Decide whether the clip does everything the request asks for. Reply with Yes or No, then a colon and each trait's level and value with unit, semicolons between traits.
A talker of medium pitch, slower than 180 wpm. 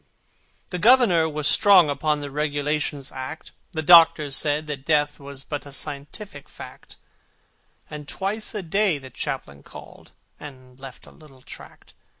Yes: medium, 150 Hz; average, 150 wpm